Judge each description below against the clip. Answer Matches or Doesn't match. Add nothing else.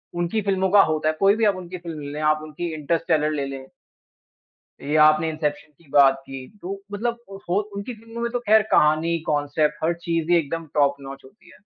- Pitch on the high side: Doesn't match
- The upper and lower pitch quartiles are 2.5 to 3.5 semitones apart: Doesn't match